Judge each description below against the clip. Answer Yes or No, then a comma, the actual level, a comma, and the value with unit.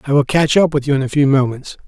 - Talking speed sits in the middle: No, fast, 320 wpm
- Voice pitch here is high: No, medium, 140 Hz